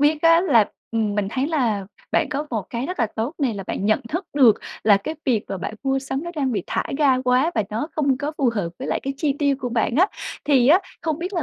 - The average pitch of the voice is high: Yes, very high, 270 Hz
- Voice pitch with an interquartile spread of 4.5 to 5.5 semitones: Yes, average, 5.1 semitones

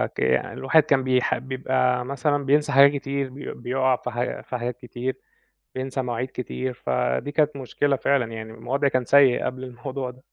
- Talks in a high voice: No, low, 130 Hz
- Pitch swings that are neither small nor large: No, narrow, 2.0 semitones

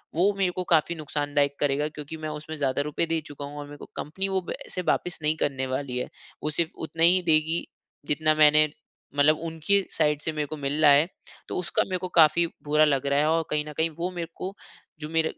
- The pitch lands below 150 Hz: No, medium, 155 Hz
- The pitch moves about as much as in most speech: No, narrow, 2.1 semitones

